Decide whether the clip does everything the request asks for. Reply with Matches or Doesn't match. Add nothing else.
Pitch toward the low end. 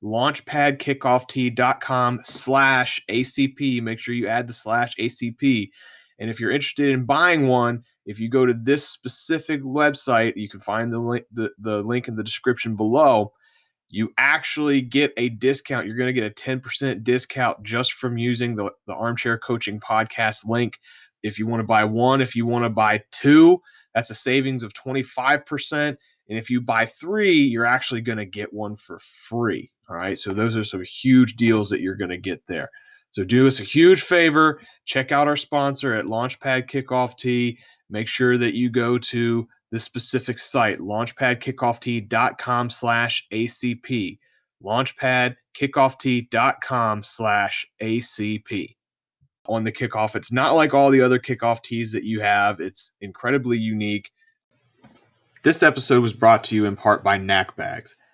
Matches